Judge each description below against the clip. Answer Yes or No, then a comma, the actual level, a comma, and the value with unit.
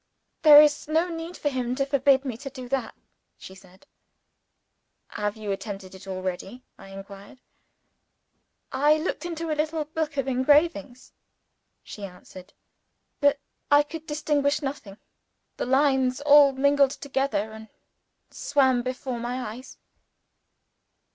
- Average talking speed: No, slow, 130 wpm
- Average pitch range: Yes, average, 5.0 semitones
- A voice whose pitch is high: Yes, very high, 270 Hz